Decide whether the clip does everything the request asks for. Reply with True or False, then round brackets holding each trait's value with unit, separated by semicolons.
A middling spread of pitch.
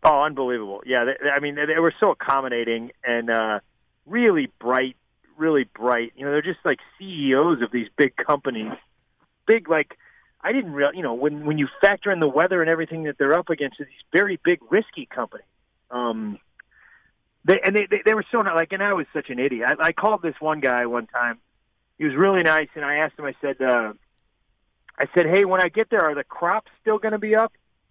False (7.0 semitones)